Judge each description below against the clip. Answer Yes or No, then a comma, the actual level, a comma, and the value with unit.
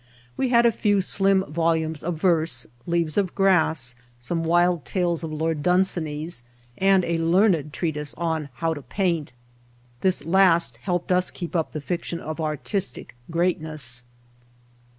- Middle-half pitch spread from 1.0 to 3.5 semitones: Yes, average, 2.8 semitones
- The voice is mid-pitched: Yes, medium, 165 Hz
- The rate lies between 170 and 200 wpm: No, average, 150 wpm